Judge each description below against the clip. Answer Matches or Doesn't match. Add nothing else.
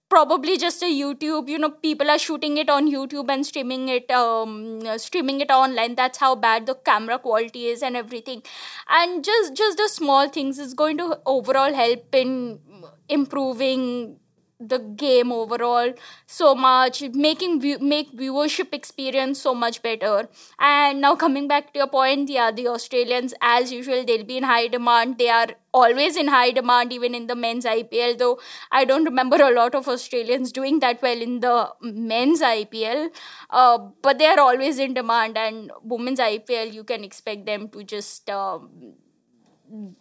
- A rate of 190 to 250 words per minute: Doesn't match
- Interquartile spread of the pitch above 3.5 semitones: Doesn't match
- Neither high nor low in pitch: Doesn't match